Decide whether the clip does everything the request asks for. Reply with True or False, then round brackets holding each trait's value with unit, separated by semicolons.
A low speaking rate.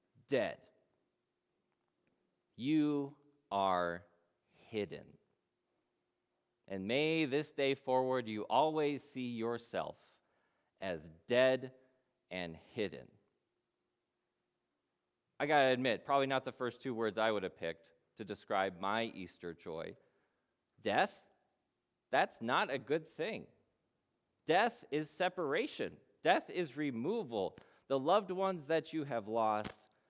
True (110 wpm)